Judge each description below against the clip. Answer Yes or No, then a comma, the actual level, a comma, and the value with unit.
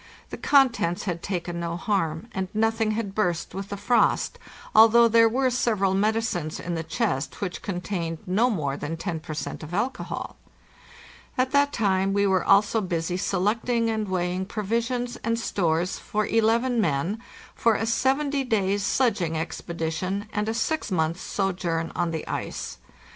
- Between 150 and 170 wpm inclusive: Yes, average, 160 wpm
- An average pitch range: Yes, average, 4.7 semitones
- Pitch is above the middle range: Yes, high, 200 Hz